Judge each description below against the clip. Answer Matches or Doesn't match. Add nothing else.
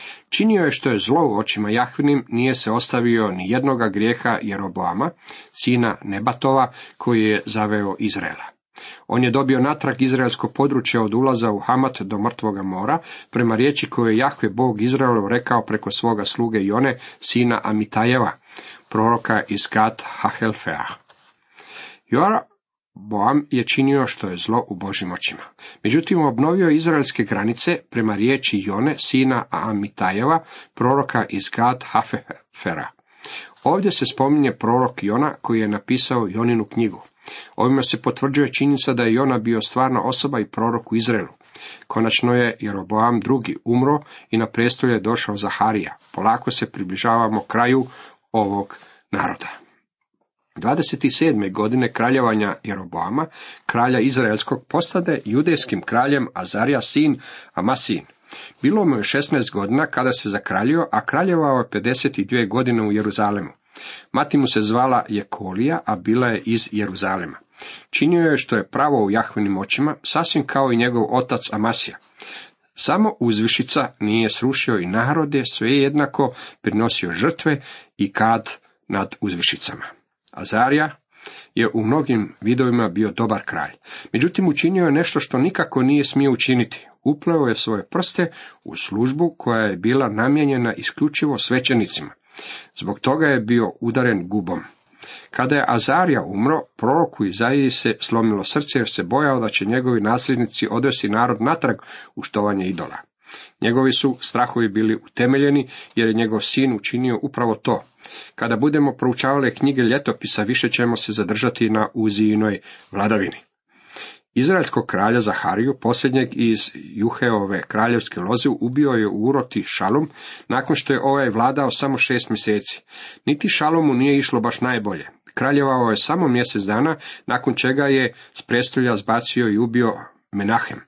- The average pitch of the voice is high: Doesn't match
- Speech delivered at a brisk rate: Doesn't match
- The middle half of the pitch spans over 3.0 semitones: Matches